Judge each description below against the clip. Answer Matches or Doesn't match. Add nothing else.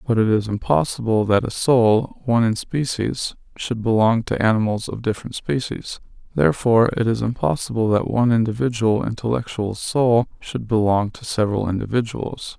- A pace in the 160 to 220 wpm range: Doesn't match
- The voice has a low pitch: Matches